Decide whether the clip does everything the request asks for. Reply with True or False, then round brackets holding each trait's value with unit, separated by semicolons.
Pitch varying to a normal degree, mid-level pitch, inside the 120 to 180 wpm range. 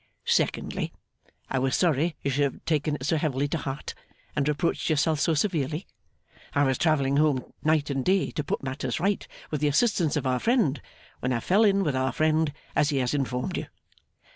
False (3.2 semitones; 150 Hz; 195 wpm)